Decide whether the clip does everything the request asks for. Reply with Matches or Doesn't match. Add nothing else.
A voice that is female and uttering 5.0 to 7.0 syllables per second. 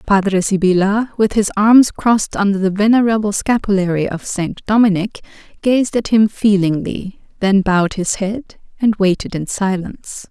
Doesn't match